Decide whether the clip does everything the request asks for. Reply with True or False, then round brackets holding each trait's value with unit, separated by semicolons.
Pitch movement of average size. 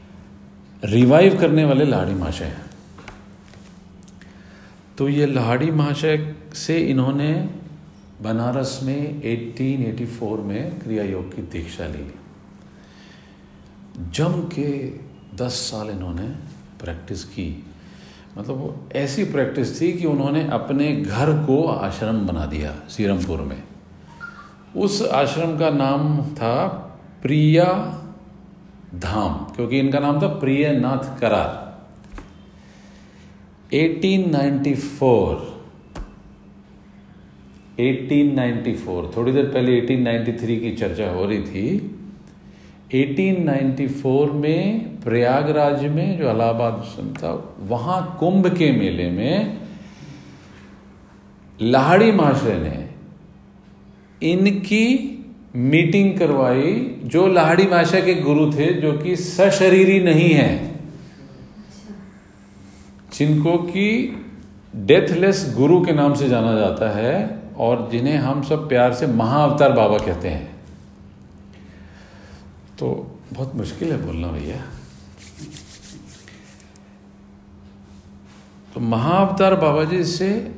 False (8.2 semitones)